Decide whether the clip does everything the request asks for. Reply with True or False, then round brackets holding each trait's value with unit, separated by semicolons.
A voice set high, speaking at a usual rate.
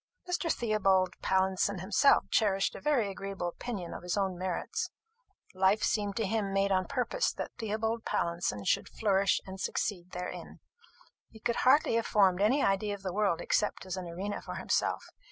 True (195 Hz; 170 wpm)